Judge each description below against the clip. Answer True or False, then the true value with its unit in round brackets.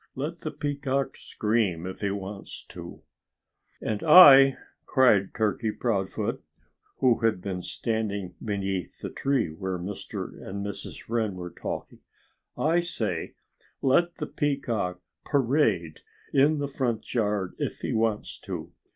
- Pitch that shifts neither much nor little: False (5.8 semitones)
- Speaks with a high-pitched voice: False (110 Hz)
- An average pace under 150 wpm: True (135 wpm)